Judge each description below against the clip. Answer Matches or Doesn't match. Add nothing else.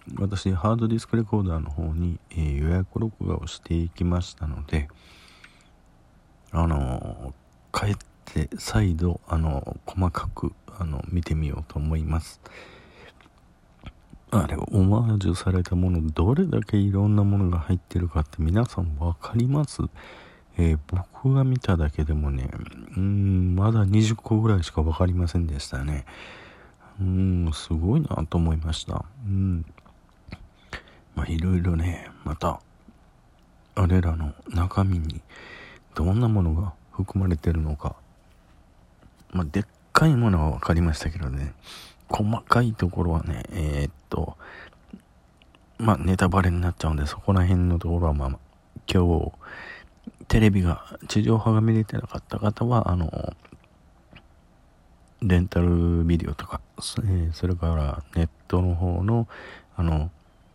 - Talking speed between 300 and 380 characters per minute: Doesn't match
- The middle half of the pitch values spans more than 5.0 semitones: Doesn't match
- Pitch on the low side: Matches